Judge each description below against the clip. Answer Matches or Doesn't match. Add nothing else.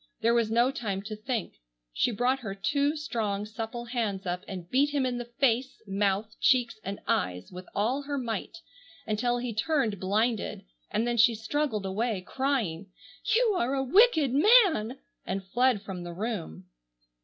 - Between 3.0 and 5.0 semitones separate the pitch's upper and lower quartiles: Matches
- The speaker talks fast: Doesn't match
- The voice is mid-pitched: Doesn't match